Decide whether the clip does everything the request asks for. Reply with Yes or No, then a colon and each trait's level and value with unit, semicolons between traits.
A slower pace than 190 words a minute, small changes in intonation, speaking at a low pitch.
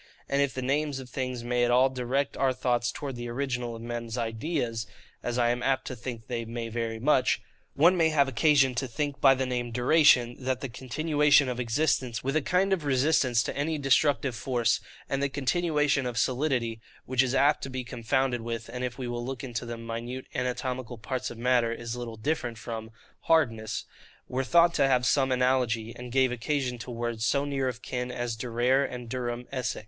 No: fast, 205 wpm; narrow, 2.3 semitones; low, 125 Hz